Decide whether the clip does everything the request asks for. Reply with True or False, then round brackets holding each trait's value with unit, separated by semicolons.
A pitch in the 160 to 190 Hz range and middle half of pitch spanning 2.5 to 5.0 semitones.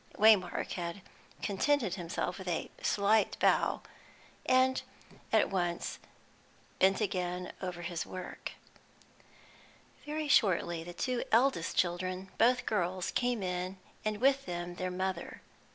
True (185 Hz; 3.8 semitones)